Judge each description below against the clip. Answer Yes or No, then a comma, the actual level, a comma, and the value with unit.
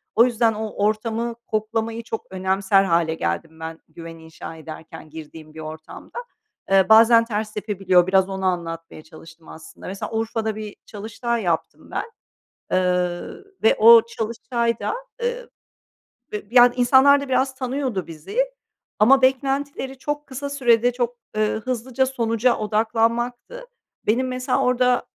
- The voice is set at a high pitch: Yes, high, 220 Hz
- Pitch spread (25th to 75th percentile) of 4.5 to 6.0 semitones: Yes, average, 5.0 semitones